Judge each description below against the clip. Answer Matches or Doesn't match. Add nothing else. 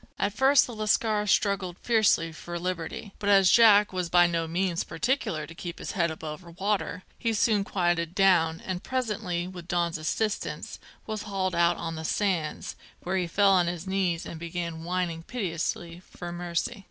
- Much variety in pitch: Doesn't match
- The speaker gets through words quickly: Doesn't match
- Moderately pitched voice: Matches